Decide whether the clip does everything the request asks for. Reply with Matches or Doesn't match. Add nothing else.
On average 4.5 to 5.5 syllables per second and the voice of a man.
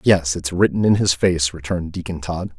Matches